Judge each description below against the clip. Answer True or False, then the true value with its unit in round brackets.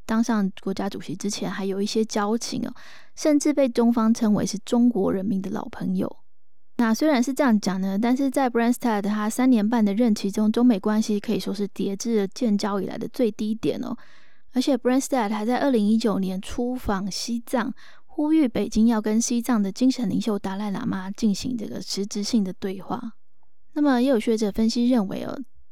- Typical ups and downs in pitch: True (3.3 semitones)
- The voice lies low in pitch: False (225 Hz)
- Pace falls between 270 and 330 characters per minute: True (320 characters per minute)